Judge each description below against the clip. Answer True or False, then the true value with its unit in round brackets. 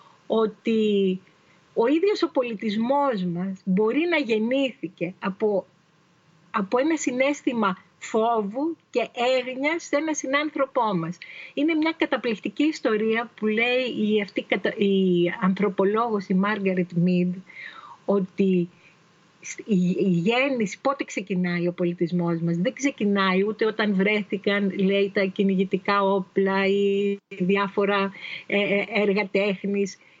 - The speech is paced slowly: True (105 wpm)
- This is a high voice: True (200 Hz)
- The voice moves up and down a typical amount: True (4.3 semitones)